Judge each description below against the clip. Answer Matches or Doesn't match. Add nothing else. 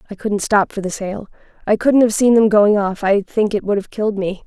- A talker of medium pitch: Doesn't match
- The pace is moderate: Doesn't match